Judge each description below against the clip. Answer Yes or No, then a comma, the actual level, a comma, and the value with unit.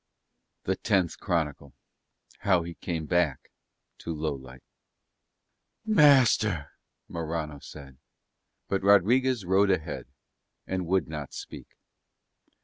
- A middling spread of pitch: Yes, average, 4.4 semitones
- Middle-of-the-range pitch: No, very low, 85 Hz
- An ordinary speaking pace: No, slow, 95 wpm